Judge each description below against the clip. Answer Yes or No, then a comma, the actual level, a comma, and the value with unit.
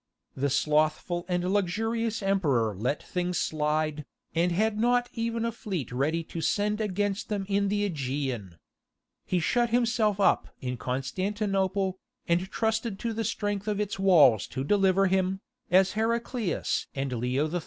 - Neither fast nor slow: Yes, average, 150 wpm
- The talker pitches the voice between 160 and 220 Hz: Yes, high, 190 Hz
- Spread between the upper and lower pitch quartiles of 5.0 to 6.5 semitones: Yes, wide, 5.5 semitones